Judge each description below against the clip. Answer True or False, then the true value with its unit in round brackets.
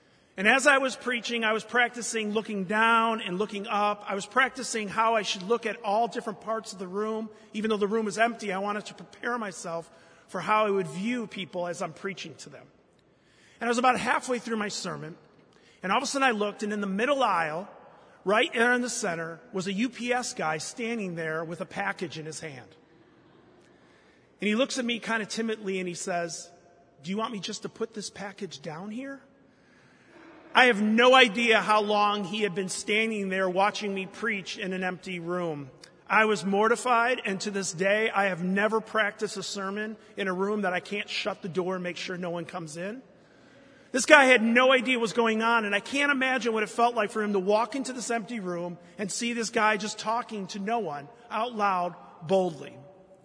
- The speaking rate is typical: False (215 wpm)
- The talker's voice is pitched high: True (210 Hz)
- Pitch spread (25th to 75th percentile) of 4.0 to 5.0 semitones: False (3.5 semitones)